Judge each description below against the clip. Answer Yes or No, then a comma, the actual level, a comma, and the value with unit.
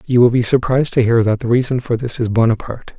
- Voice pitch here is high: No, low, 120 Hz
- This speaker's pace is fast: Yes, fast, 260 wpm